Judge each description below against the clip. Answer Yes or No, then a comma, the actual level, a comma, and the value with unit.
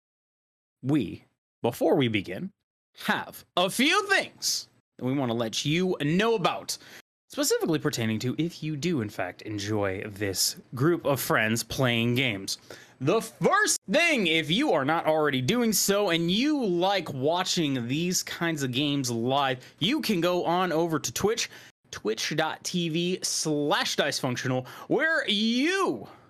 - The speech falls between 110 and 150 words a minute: Yes, average, 140 wpm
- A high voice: No, medium, 160 Hz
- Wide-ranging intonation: Yes, wide, 6.7 semitones